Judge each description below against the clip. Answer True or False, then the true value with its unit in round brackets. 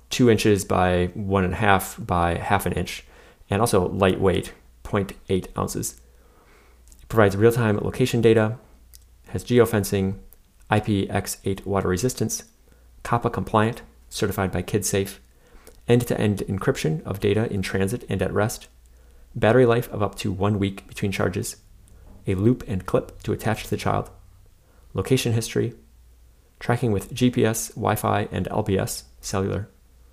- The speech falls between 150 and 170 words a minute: False (135 wpm)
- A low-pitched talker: True (100 Hz)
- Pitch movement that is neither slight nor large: True (3.2 semitones)